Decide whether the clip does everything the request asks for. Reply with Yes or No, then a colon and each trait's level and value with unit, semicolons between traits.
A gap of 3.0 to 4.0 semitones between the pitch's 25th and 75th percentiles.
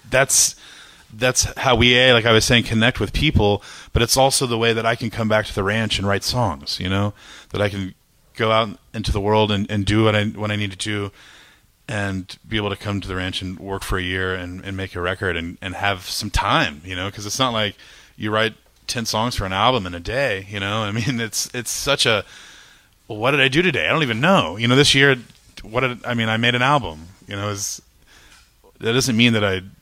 Yes: average, 3.5 semitones